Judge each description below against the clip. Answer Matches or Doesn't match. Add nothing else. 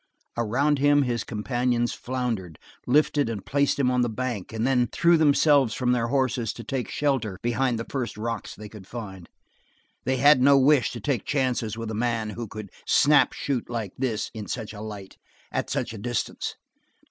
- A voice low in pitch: Matches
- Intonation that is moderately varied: Matches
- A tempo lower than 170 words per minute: Doesn't match